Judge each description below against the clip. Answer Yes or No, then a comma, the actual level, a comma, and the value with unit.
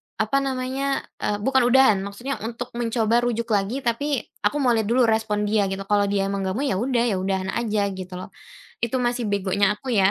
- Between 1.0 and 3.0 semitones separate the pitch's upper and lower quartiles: No, average, 3.7 semitones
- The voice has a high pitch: Yes, high, 225 Hz